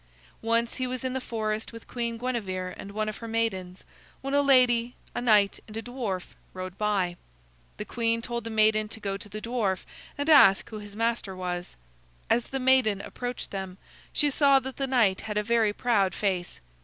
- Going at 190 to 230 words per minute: Yes, average, 195 wpm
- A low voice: No, high, 225 Hz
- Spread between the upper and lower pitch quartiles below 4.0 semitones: Yes, average, 3.6 semitones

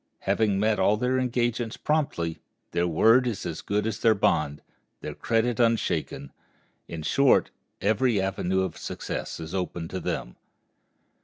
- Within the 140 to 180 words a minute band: Yes, average, 145 wpm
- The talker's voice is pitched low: Yes, low, 105 Hz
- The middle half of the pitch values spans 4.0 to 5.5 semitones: Yes, average, 4.7 semitones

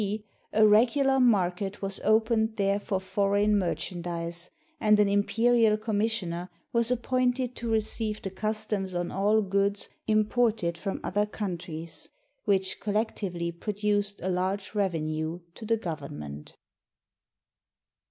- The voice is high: Yes, high, 205 Hz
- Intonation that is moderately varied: Yes, average, 3.2 semitones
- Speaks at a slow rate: Yes, slow, 125 wpm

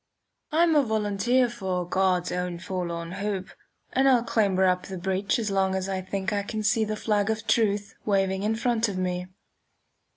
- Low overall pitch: No, high, 200 Hz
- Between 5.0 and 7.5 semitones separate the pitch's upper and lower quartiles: No, average, 2.8 semitones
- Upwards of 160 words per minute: Yes, average, 185 wpm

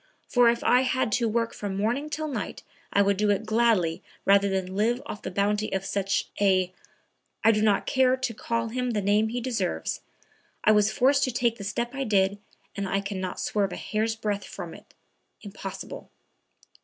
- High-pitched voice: Yes, high, 215 Hz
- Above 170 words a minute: Yes, average, 200 wpm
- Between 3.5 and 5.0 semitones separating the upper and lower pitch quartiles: No, average, 3.1 semitones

